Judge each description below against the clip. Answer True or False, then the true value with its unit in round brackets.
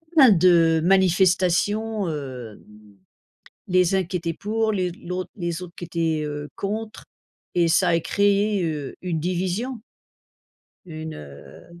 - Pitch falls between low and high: True (180 Hz)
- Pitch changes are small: False (3.2 semitones)